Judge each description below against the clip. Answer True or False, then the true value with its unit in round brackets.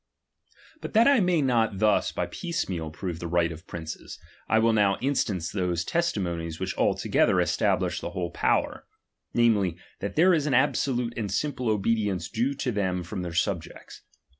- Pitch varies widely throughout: True (6.5 semitones)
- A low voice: True (105 Hz)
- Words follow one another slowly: False (175 wpm)